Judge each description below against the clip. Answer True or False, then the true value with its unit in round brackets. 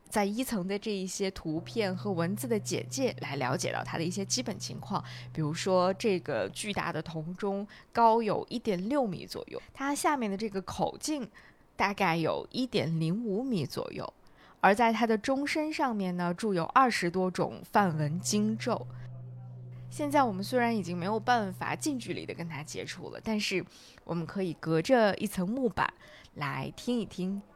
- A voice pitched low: False (195 Hz)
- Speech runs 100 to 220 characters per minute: False (260 characters per minute)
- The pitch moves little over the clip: False (5.3 semitones)